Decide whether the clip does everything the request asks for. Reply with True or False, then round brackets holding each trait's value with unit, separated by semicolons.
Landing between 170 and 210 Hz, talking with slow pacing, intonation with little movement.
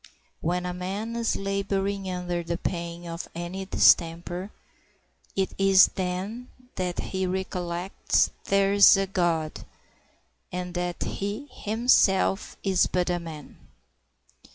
True (185 Hz; 120 wpm; 2.0 semitones)